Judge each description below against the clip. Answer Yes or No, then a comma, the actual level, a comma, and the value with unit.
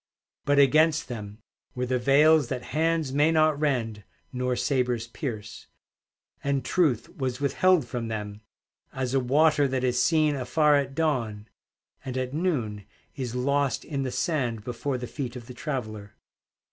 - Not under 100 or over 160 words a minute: Yes, average, 155 wpm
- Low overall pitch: Yes, low, 130 Hz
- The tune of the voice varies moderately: Yes, average, 3.4 semitones